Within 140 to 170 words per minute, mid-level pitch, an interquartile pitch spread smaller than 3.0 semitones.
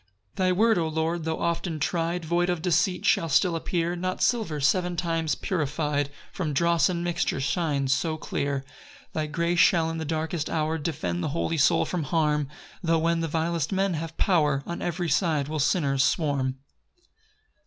No: average, 180 wpm; medium, 165 Hz; narrow, 2.5 semitones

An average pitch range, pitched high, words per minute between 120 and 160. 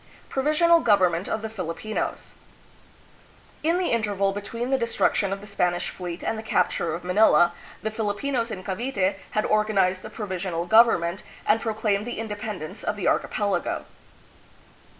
Yes: average, 3.4 semitones; high, 205 Hz; average, 150 wpm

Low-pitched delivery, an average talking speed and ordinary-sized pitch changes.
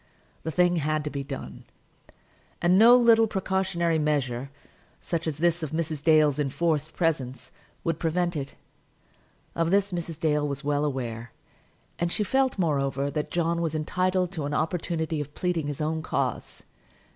No: medium, 160 Hz; average, 155 wpm; average, 3.1 semitones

